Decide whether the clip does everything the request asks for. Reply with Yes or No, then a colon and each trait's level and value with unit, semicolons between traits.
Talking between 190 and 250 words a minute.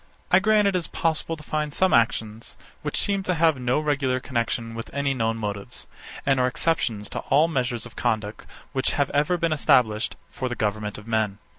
Yes: average, 200 wpm